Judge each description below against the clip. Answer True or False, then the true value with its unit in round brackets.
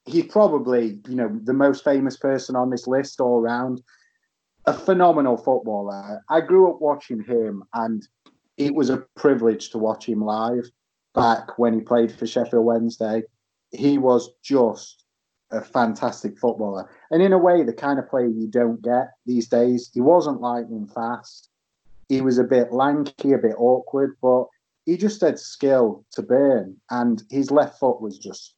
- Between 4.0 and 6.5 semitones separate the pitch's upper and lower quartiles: False (3.3 semitones)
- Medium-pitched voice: False (125 Hz)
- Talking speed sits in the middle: True (170 wpm)